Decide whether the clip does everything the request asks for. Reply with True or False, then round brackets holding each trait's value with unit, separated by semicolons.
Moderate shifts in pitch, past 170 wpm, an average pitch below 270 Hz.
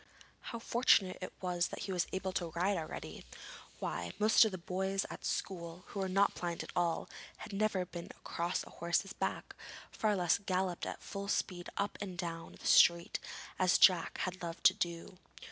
False (2.2 semitones; 185 wpm; 185 Hz)